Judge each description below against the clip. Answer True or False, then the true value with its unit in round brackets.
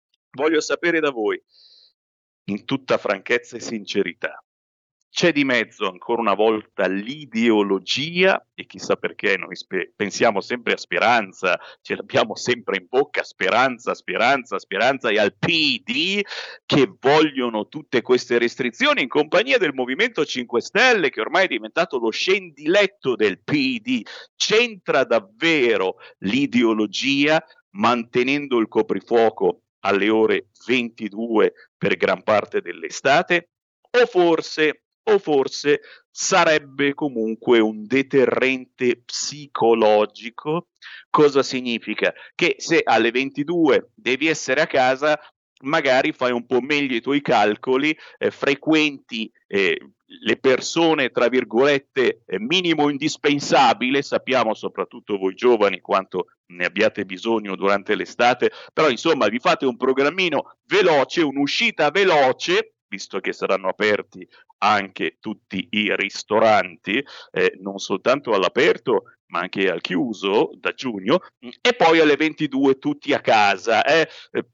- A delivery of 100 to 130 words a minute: True (120 wpm)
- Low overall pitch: False (150 Hz)